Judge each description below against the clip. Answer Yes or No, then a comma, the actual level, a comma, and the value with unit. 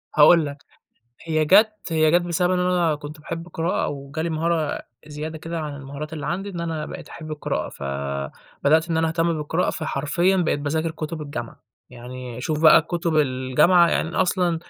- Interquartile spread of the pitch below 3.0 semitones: Yes, narrow, 2.5 semitones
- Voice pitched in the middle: Yes, medium, 160 Hz